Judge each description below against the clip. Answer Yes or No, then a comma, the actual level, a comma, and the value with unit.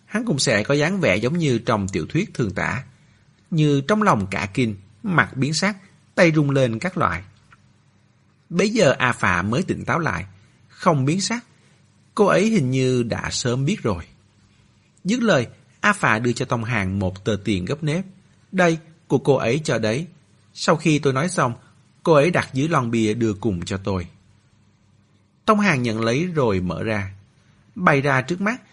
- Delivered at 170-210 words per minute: Yes, average, 190 wpm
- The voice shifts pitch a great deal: Yes, wide, 7.0 semitones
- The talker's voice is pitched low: Yes, low, 130 Hz